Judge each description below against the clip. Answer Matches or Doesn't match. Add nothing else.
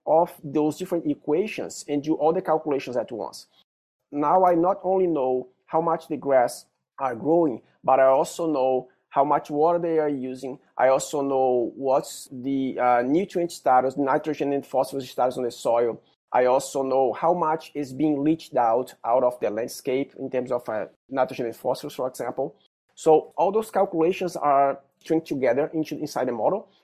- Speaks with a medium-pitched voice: Matches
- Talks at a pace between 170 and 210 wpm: Matches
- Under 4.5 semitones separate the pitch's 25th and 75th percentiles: Matches